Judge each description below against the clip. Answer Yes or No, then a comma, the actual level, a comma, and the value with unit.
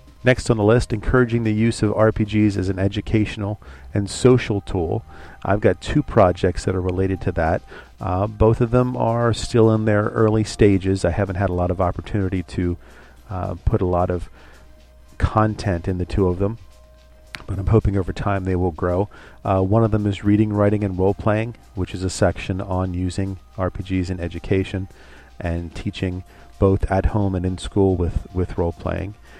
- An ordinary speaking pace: Yes, average, 190 wpm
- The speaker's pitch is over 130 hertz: No, very low, 95 Hz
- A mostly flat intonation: No, average, 3.1 semitones